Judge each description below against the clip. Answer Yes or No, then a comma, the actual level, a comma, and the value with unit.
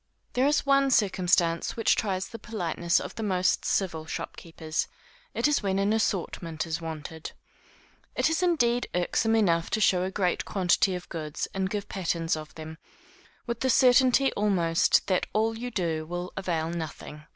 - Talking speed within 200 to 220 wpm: No, average, 165 wpm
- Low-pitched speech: No, medium, 185 Hz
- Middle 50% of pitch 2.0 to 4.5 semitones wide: No, average, 5.1 semitones